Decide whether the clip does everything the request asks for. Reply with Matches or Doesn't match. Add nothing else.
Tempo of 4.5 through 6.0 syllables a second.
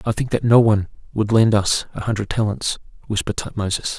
Doesn't match